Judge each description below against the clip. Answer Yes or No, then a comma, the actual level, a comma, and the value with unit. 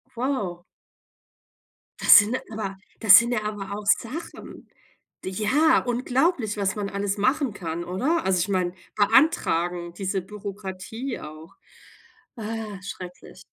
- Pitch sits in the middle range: No, high, 205 Hz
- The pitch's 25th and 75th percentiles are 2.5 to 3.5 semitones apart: No, average, 4.0 semitones